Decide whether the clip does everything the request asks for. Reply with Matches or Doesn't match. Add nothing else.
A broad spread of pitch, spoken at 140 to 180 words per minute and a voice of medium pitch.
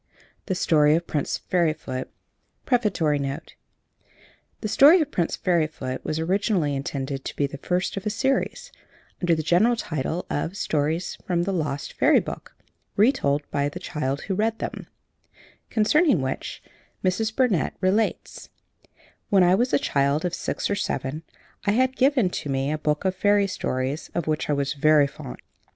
Matches